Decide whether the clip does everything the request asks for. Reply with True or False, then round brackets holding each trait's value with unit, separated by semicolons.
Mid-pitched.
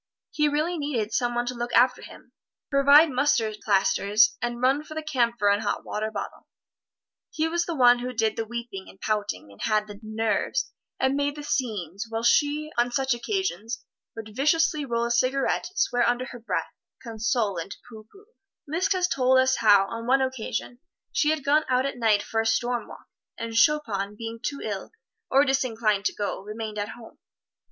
False (240 Hz)